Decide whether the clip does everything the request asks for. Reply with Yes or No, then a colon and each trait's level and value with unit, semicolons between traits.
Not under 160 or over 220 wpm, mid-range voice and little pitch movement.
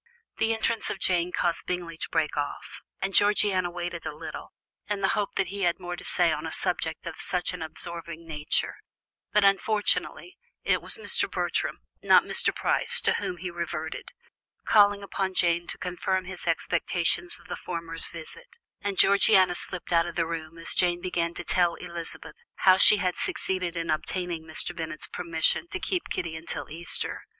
Yes: average, 180 wpm; medium, 175 Hz; narrow, 2.3 semitones